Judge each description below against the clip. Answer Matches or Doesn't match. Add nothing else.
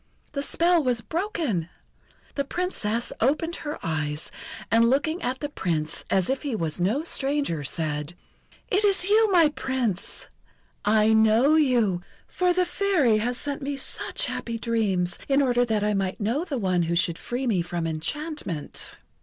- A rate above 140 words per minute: Matches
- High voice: Matches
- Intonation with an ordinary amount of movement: Doesn't match